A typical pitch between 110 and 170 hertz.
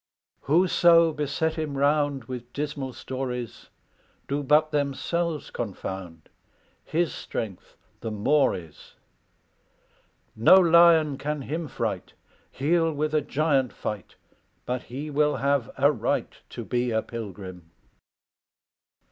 Yes: medium, 140 Hz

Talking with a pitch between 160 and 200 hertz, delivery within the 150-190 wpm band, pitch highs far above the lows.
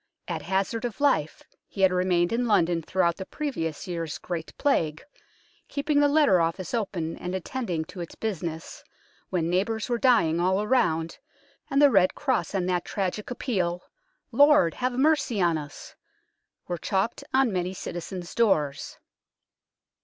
Yes: high, 190 Hz; average, 160 wpm; wide, 5.8 semitones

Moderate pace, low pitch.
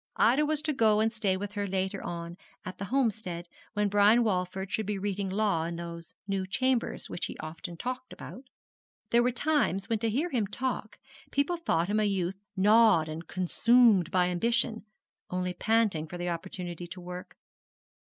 No: average, 180 wpm; high, 200 Hz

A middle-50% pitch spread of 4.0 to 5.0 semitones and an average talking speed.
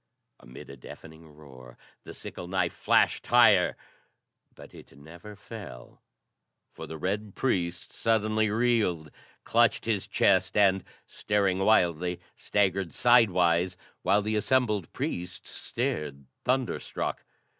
No: average, 4.3 semitones; slow, 115 wpm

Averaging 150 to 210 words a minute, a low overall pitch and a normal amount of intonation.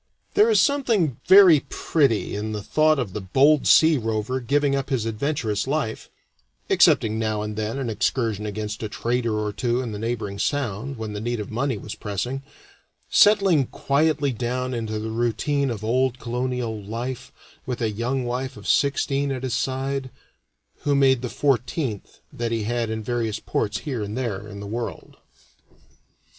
Yes: average, 170 wpm; low, 120 Hz; average, 4.0 semitones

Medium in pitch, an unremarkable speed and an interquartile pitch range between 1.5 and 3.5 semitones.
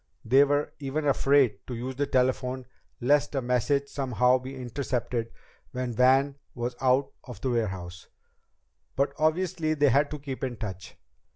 No: low, 130 Hz; average, 155 wpm; narrow, 2.5 semitones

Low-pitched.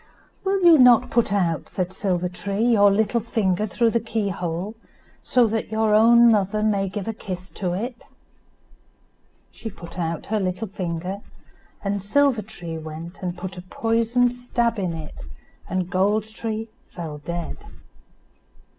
No: high, 200 Hz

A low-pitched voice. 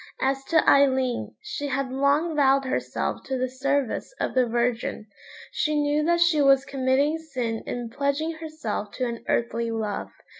No: very high, 270 Hz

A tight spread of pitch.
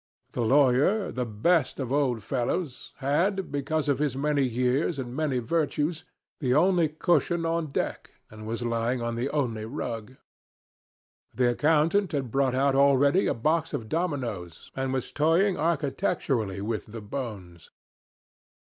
No: average, 4.7 semitones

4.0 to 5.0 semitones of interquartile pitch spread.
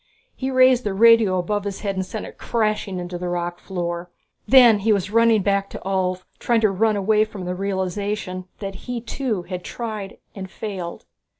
No: average, 3.1 semitones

